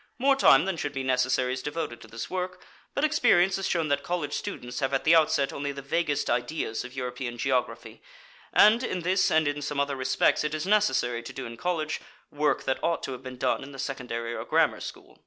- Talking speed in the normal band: No, fast, 225 wpm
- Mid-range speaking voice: Yes, medium, 145 Hz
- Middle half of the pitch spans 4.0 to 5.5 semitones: Yes, average, 5.0 semitones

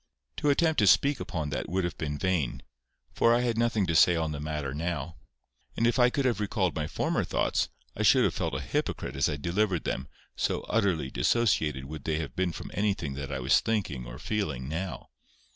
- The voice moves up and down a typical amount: No, wide, 6.6 semitones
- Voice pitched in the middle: No, very low, 85 Hz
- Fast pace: Yes, fast, 210 wpm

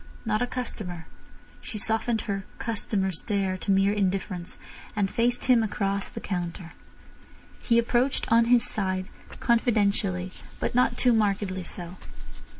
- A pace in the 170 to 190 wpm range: No, slow, 135 wpm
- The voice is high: Yes, high, 205 Hz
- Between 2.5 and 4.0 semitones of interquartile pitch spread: Yes, average, 3.6 semitones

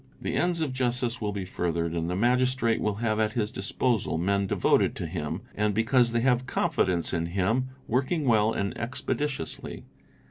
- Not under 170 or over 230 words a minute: Yes, average, 180 wpm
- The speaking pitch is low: Yes, low, 110 Hz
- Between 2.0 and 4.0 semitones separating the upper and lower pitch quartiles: No, average, 4.8 semitones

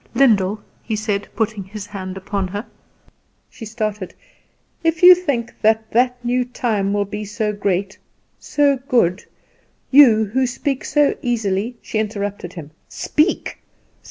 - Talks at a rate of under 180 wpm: Yes, average, 140 wpm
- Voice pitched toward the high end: Yes, high, 215 Hz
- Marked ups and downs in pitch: No, average, 3.7 semitones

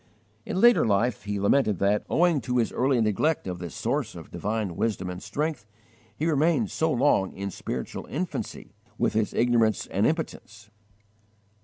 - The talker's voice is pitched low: Yes, low, 115 Hz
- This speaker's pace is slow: No, average, 160 wpm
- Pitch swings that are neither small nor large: No, wide, 7.0 semitones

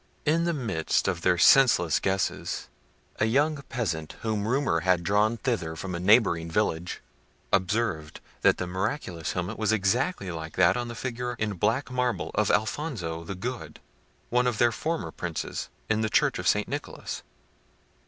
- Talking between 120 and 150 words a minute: No, average, 165 wpm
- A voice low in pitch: Yes, low, 105 Hz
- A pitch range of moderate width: No, wide, 5.8 semitones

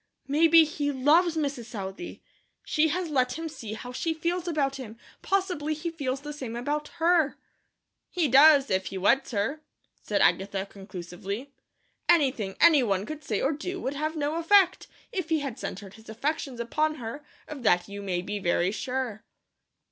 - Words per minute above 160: Yes, average, 170 wpm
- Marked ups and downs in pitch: Yes, wide, 6.3 semitones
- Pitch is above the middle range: Yes, very high, 275 Hz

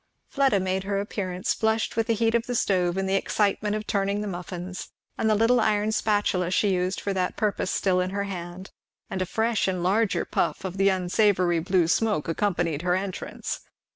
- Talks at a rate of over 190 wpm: Yes, average, 200 wpm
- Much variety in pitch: No, narrow, 2.6 semitones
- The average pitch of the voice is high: Yes, high, 195 Hz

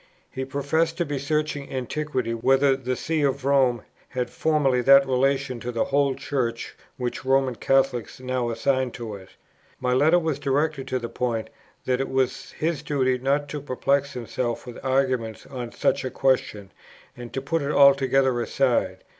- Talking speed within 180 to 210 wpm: No, average, 170 wpm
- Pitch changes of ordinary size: No, narrow, 2.0 semitones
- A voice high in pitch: No, low, 135 Hz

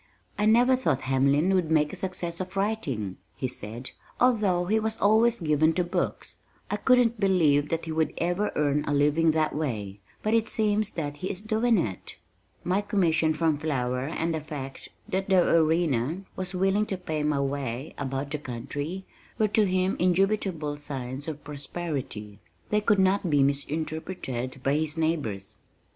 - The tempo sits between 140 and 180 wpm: Yes, average, 170 wpm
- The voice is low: No, medium, 160 Hz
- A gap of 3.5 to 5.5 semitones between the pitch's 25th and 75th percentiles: Yes, average, 5.2 semitones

